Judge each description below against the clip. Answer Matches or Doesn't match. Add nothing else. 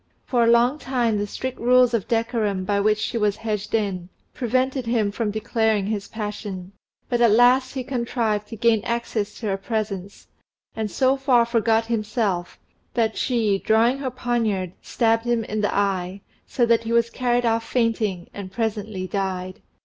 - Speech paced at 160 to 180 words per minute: Matches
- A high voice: Matches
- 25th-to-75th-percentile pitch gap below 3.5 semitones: Matches